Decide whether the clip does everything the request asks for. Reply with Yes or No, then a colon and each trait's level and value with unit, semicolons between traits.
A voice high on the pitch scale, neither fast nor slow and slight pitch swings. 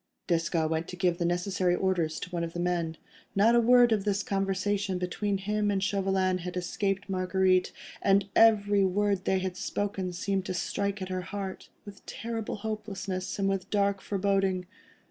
Yes: high, 195 Hz; average, 170 wpm; narrow, 1.8 semitones